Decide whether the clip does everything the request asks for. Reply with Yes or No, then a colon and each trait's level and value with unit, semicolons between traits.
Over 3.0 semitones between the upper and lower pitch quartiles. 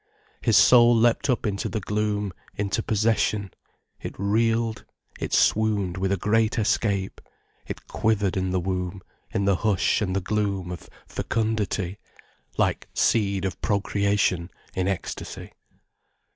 No: narrow, 2.4 semitones